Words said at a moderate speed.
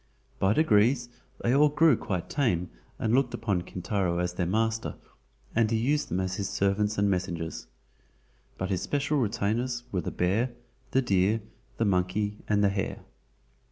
Yes: average, 160 wpm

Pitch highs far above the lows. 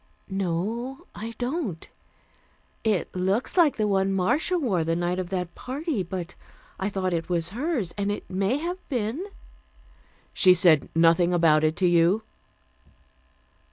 Yes: wide, 5.8 semitones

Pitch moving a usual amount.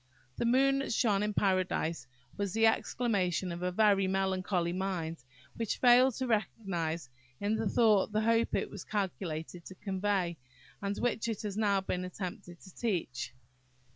Yes: average, 3.5 semitones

